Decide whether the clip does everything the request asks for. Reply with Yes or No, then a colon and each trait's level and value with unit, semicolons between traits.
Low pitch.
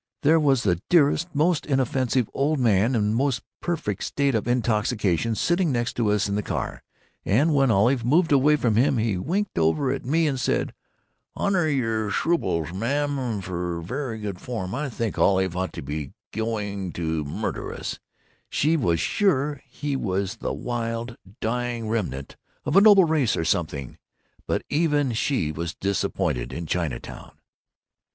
Yes: low, 115 Hz